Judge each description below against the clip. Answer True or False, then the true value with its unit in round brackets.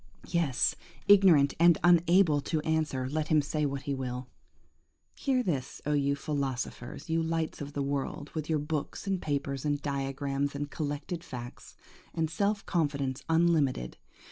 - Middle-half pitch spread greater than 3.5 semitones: False (2.8 semitones)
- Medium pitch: True (145 Hz)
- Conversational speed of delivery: True (145 wpm)